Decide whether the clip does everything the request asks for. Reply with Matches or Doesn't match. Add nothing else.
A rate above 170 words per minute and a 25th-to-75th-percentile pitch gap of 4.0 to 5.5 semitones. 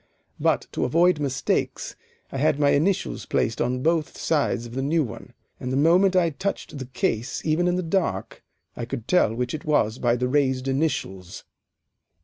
Matches